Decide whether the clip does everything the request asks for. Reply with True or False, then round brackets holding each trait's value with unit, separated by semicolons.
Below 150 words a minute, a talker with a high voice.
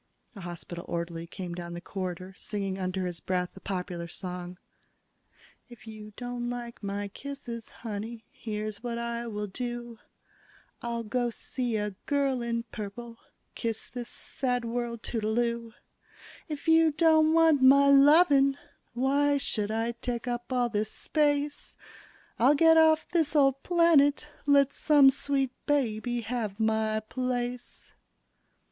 True (140 wpm; 235 Hz)